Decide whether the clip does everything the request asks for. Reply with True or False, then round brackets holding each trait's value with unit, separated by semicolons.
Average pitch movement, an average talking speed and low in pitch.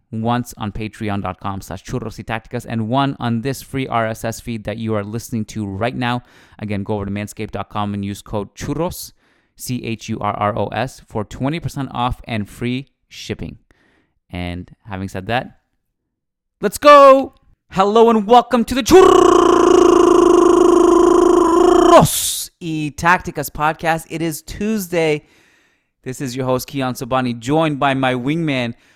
False (8.1 semitones; 145 wpm; 130 Hz)